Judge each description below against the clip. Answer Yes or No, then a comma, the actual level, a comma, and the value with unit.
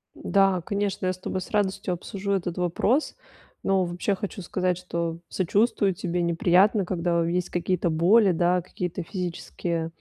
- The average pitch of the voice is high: No, medium, 180 Hz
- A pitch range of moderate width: No, narrow, 2.1 semitones